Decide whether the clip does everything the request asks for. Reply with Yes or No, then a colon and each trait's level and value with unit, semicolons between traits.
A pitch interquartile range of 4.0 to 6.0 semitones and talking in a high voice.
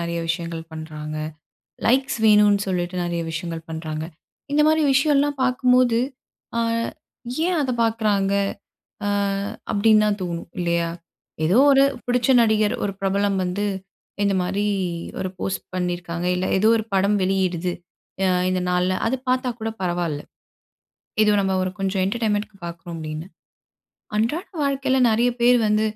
Yes: average, 4.5 semitones; high, 195 Hz